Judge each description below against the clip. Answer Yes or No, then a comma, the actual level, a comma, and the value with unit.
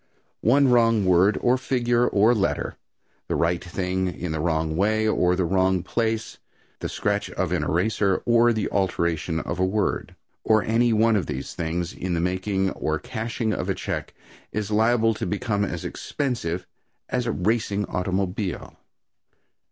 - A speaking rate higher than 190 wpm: No, average, 160 wpm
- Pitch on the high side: No, low, 100 Hz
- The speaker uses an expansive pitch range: No, average, 4.0 semitones